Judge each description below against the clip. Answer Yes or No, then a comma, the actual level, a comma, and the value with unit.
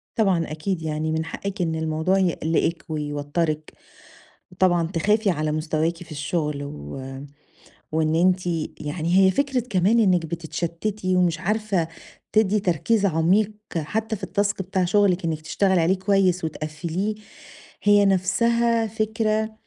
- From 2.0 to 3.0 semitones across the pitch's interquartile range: No, average, 4.2 semitones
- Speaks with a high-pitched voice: No, medium, 180 Hz